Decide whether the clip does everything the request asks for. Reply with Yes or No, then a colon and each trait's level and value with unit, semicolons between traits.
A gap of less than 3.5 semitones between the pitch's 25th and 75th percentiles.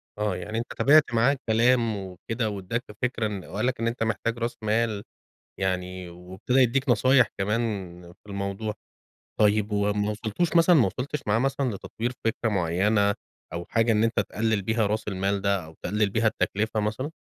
Yes: average, 2.8 semitones